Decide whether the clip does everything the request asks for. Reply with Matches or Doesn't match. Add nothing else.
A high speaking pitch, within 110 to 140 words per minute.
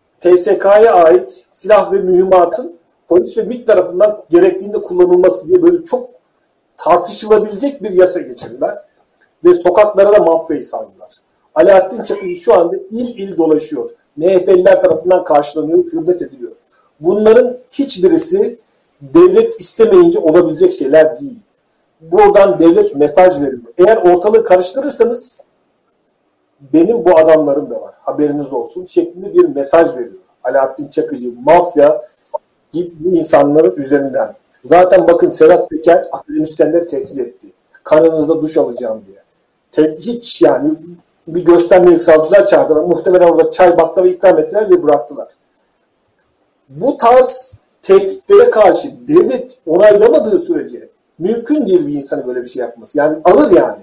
Matches